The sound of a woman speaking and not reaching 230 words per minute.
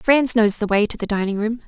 No: female; fast, 285 wpm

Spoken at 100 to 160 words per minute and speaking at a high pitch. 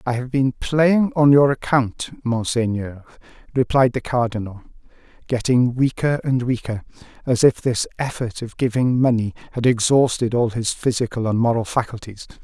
No: average, 145 wpm; low, 120 Hz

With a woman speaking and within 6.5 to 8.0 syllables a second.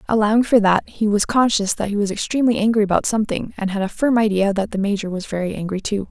Yes: female; 6.7 syllables/s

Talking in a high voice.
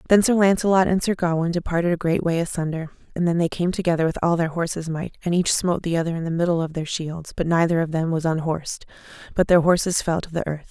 No: medium, 170 Hz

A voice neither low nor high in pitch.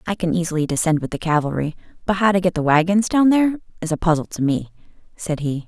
Yes: medium, 175 Hz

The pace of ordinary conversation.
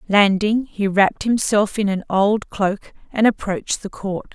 Yes: average, 165 wpm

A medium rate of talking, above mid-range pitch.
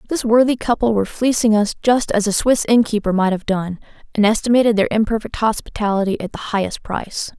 Yes: average, 185 wpm; high, 215 Hz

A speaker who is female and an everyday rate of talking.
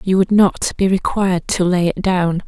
No: female; fast, 220 wpm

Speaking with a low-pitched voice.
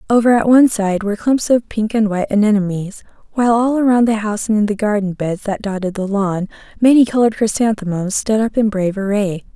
No: high, 215 Hz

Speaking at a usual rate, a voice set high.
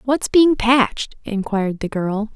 Yes: average, 155 wpm; high, 230 Hz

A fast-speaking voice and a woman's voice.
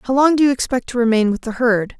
Yes: fast, 300 wpm; female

